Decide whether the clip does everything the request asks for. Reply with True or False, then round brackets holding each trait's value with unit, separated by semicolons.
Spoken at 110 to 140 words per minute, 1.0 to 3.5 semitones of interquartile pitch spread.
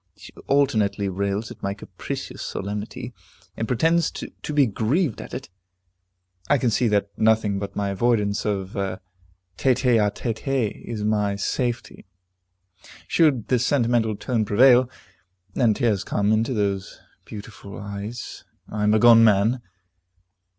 True (135 wpm; 3.2 semitones)